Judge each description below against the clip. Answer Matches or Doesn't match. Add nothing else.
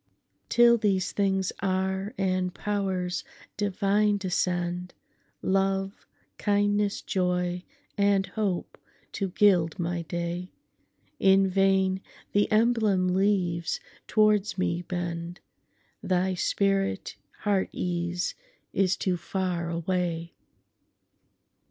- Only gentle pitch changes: Matches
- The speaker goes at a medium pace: Doesn't match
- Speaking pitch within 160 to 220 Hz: Matches